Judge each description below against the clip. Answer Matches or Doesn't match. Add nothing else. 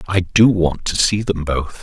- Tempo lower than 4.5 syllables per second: Matches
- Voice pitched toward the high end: Doesn't match